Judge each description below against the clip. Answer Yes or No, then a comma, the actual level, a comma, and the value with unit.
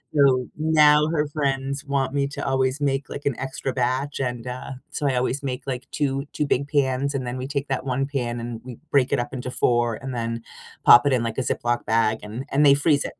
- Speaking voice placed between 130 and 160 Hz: Yes, low, 135 Hz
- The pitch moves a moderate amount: No, narrow, 2.2 semitones